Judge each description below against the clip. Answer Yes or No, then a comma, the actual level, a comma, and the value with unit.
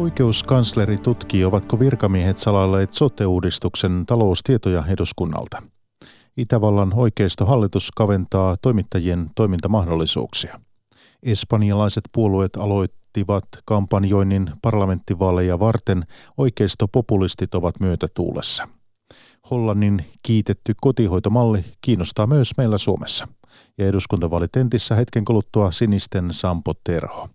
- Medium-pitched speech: No, low, 105 Hz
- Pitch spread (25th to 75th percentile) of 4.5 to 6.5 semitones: No, average, 3.3 semitones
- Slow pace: Yes, slow, 80 wpm